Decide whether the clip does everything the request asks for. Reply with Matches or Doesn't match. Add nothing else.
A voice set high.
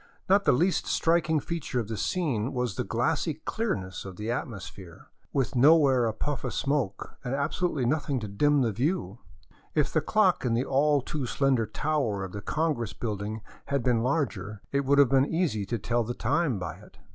Doesn't match